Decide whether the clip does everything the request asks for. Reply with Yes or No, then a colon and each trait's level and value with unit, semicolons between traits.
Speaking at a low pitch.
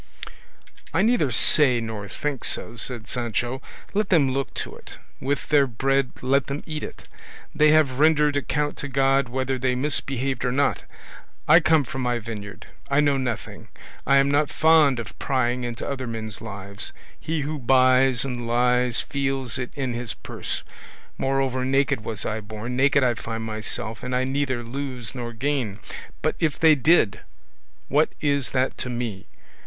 Yes: low, 130 Hz